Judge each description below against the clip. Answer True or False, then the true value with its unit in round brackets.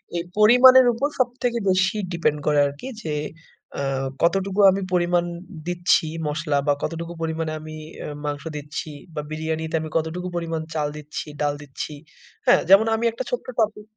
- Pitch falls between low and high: True (170 Hz)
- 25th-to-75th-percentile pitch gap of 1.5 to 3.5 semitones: False (4.3 semitones)